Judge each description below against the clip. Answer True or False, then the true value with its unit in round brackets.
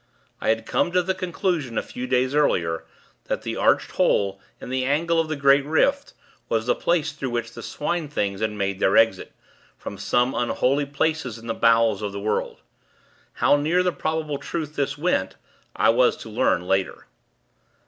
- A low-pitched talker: True (130 Hz)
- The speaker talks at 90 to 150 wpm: False (185 wpm)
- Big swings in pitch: True (6.0 semitones)